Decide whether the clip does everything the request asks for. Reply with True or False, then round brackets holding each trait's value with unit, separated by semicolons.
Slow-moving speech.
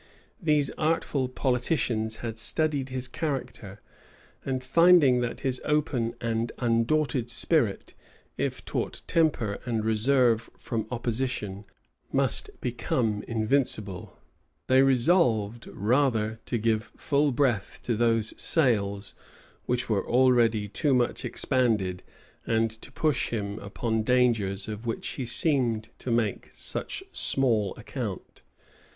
True (115 wpm)